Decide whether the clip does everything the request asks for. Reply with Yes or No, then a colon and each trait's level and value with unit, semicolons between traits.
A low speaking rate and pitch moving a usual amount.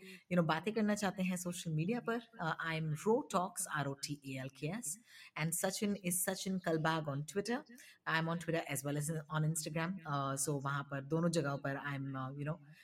No: average, 185 wpm; average, 4.6 semitones